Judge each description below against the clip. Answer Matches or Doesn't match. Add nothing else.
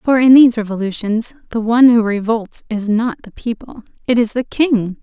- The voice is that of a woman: Matches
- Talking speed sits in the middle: Matches